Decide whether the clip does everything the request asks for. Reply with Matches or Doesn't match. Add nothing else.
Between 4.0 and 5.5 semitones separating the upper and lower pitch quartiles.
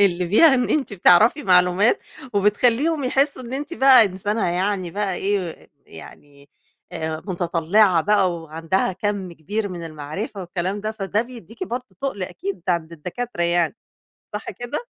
Matches